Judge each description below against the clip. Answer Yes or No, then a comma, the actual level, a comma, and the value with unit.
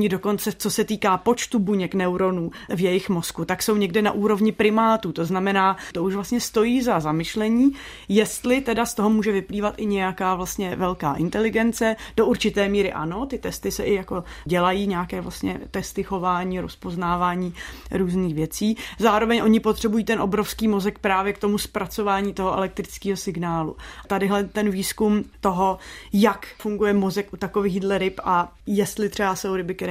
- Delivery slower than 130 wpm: No, average, 165 wpm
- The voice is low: No, high, 200 Hz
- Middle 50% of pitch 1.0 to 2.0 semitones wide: No, narrow, 2.5 semitones